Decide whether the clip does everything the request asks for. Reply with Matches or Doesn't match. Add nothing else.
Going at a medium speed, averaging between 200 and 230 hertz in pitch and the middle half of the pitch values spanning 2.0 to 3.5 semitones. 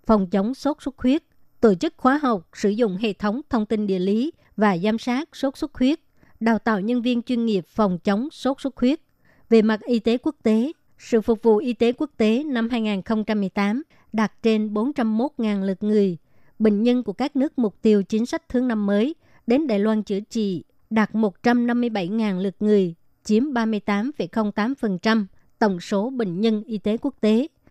Matches